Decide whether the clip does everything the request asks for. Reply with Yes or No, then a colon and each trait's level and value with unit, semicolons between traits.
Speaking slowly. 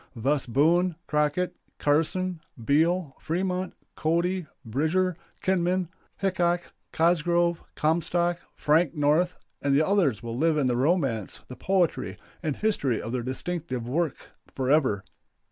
Yes: slow, 115 wpm